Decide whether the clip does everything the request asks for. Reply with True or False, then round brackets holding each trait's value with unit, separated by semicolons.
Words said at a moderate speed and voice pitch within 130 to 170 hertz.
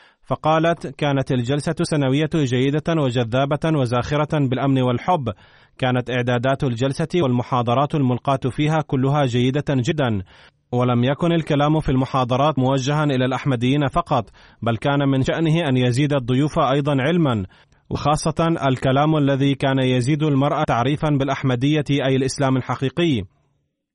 True (120 wpm; 140 Hz)